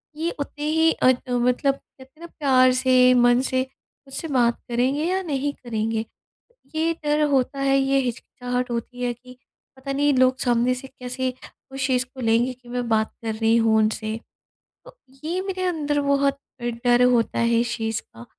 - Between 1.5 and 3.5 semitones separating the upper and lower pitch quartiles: Yes, narrow, 2.6 semitones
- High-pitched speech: Yes, very high, 255 Hz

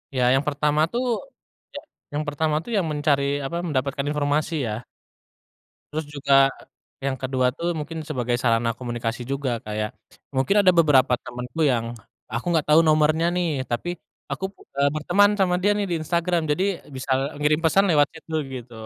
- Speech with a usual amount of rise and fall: Yes, average, 4.1 semitones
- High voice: No, medium, 150 Hz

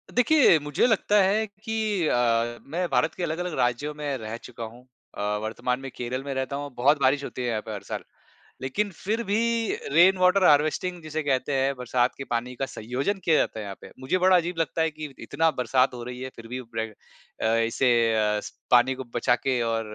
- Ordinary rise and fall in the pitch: No, wide, 6.4 semitones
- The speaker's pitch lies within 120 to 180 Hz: Yes, medium, 140 Hz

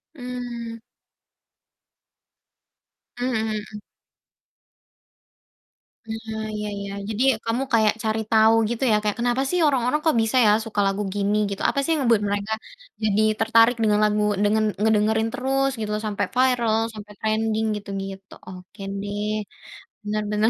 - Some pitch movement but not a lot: No, narrow, 2.0 semitones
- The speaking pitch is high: Yes, high, 220 Hz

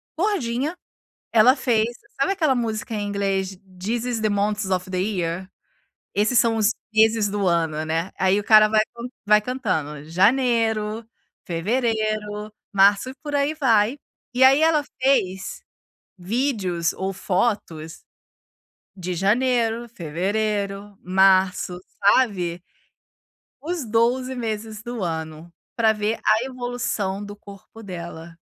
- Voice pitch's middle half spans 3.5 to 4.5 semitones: Yes, average, 3.9 semitones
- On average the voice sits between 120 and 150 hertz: No, high, 210 Hz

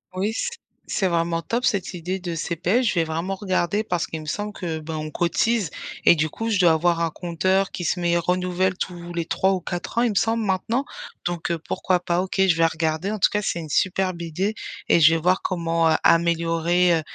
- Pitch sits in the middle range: Yes, medium, 175 Hz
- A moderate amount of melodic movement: No, narrow, 2.3 semitones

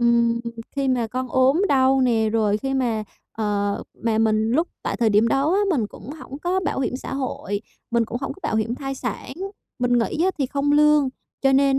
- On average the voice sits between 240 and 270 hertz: Yes, very high, 255 Hz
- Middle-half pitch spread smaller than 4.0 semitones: Yes, average, 3.5 semitones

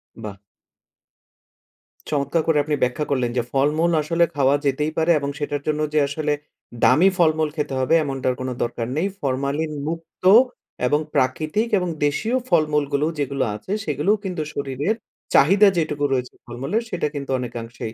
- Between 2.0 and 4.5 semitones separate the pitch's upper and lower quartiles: Yes, average, 3.2 semitones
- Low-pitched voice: No, medium, 145 Hz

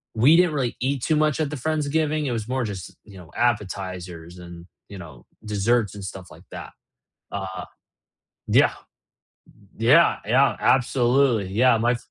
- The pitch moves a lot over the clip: Yes, wide, 6.4 semitones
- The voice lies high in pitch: No, low, 120 Hz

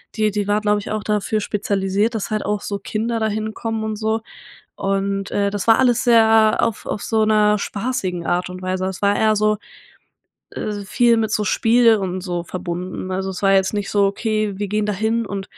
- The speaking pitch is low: No, high, 210 Hz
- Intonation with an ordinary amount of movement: No, narrow, 2.0 semitones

